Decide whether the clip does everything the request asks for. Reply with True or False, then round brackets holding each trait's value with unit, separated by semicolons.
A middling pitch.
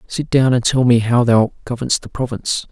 False (125 Hz)